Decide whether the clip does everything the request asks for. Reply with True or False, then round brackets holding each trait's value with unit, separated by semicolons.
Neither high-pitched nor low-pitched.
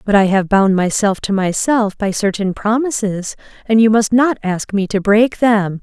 False (210 Hz)